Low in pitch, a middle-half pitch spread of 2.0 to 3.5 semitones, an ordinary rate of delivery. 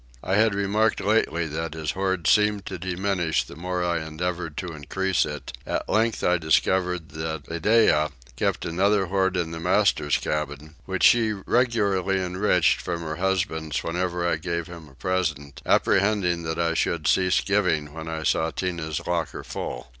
Yes: very low, 90 Hz; average, 3.1 semitones; average, 165 wpm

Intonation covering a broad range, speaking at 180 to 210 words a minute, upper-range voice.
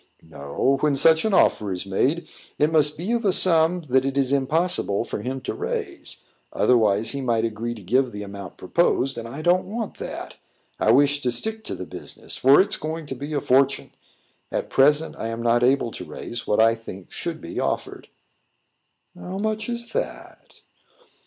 No: wide, 6.0 semitones; average, 190 wpm; low, 135 Hz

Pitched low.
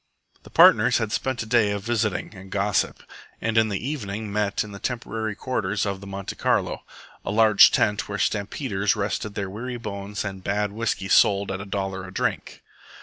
Yes: low, 105 Hz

